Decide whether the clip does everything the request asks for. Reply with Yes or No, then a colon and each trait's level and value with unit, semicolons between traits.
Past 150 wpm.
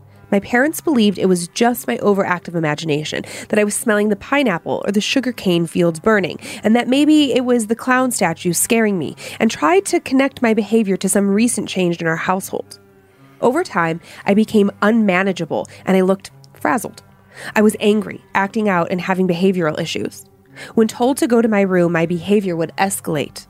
Yes: average, 185 wpm